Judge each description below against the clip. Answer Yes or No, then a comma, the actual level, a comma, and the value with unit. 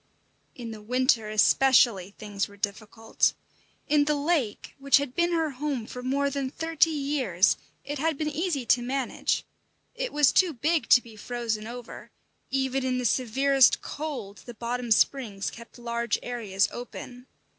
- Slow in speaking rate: No, average, 155 wpm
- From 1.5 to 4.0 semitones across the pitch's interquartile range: Yes, average, 3.7 semitones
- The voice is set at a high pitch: Yes, very high, 250 Hz